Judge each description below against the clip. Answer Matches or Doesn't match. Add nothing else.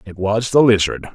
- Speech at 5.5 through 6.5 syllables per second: Doesn't match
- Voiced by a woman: Doesn't match